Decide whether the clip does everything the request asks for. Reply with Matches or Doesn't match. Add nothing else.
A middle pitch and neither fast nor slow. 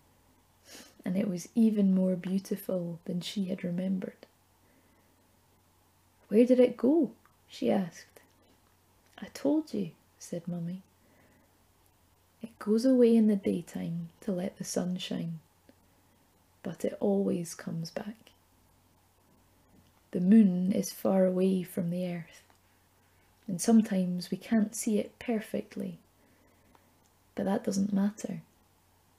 Doesn't match